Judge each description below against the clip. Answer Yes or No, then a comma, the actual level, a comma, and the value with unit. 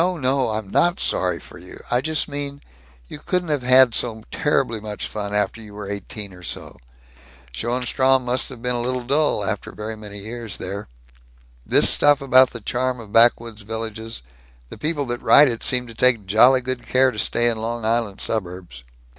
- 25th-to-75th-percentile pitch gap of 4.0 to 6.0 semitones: No, average, 3.4 semitones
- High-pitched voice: No, low, 120 Hz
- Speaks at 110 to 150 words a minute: No, average, 190 wpm